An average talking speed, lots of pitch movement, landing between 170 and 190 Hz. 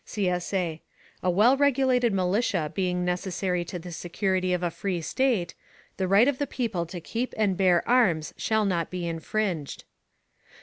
No: average, 160 wpm; average, 3.8 semitones; medium, 185 Hz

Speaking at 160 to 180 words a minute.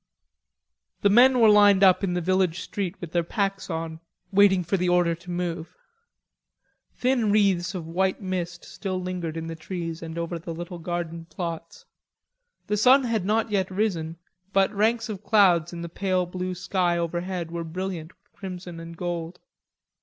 Yes: average, 170 wpm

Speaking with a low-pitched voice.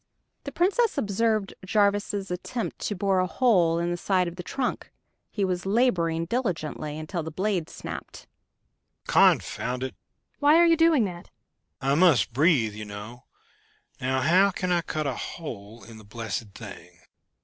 No: medium, 175 Hz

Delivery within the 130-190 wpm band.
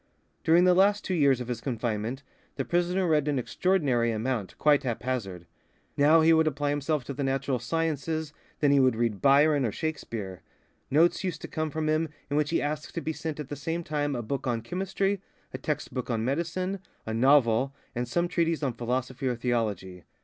No: average, 200 wpm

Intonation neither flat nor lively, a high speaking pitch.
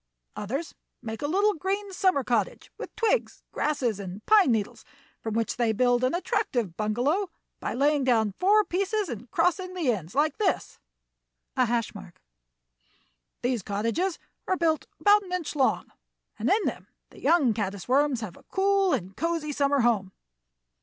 No: wide, 9.0 semitones; very high, 270 Hz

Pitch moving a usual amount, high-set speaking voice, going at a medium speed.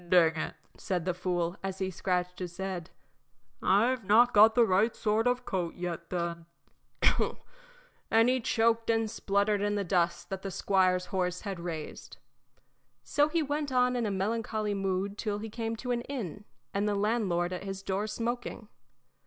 Yes: average, 3.7 semitones; high, 200 Hz; average, 170 wpm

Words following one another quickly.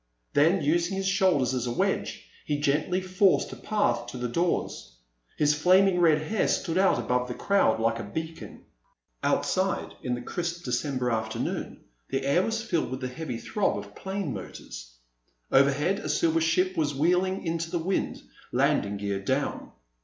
No: average, 170 wpm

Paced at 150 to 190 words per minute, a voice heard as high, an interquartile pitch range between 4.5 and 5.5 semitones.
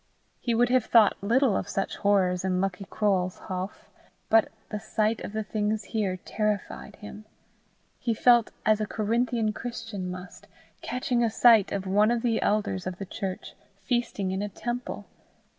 No: average, 165 wpm; high, 215 Hz; average, 2.9 semitones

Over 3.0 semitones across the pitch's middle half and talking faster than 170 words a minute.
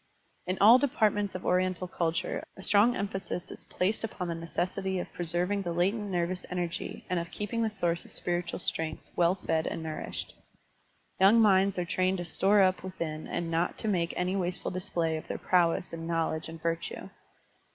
No: narrow, 2.4 semitones; average, 185 wpm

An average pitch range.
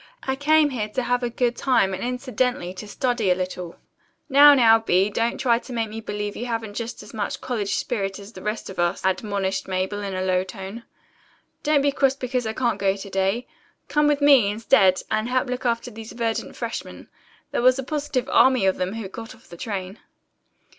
Yes: average, 4.5 semitones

